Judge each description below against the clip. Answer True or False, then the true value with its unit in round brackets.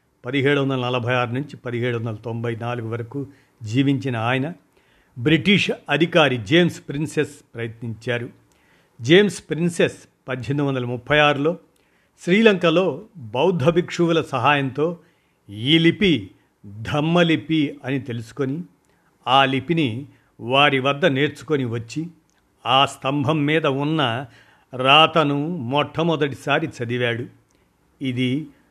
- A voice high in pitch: False (140 Hz)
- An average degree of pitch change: True (4.1 semitones)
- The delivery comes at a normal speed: True (95 wpm)